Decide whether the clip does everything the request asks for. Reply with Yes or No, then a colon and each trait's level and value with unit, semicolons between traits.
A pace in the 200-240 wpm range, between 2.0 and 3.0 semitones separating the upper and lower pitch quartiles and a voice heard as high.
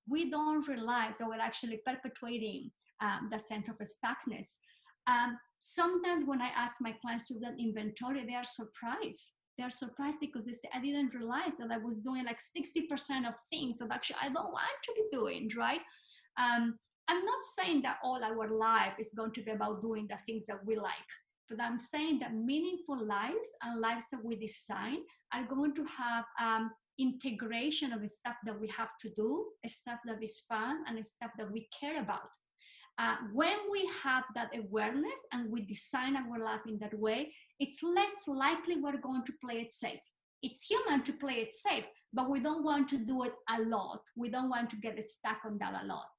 No: fast, 205 wpm; average, 4.0 semitones; high, 240 Hz